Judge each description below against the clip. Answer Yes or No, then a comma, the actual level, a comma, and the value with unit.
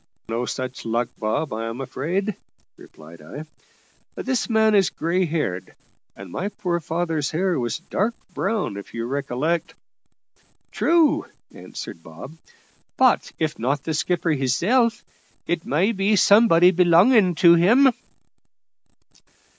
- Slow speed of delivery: Yes, slow, 125 wpm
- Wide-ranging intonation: Yes, wide, 7.2 semitones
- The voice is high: No, medium, 165 Hz